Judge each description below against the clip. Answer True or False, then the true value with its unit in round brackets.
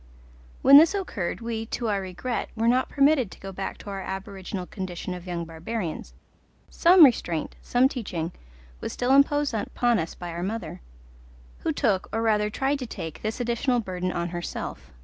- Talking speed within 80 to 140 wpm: False (175 wpm)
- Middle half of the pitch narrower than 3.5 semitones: False (5.4 semitones)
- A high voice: True (210 Hz)